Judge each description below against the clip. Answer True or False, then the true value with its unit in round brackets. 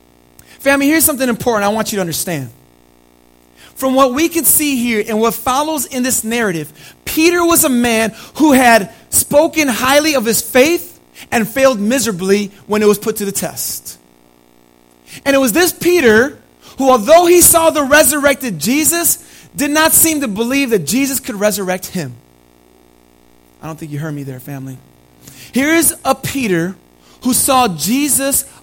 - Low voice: False (230 Hz)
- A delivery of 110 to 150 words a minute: False (165 wpm)